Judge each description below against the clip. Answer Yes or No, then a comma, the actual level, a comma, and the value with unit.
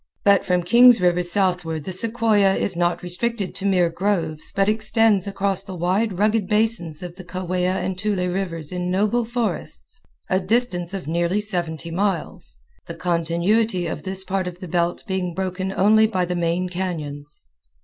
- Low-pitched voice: No, medium, 185 Hz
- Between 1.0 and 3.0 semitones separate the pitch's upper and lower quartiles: Yes, average, 2.7 semitones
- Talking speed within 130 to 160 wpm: No, average, 170 wpm